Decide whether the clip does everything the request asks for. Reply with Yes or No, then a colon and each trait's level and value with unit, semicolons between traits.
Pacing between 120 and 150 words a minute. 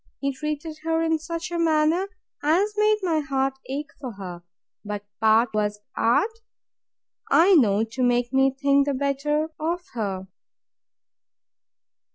Yes: average, 140 wpm